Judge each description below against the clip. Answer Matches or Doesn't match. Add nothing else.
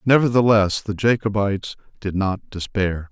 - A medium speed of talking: Doesn't match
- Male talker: Matches